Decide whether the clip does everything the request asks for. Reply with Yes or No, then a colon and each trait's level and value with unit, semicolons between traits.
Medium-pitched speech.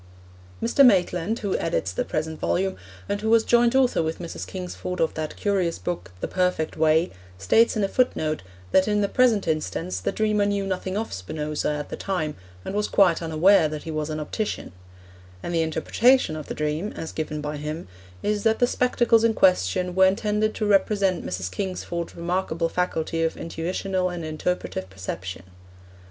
Yes: medium, 180 Hz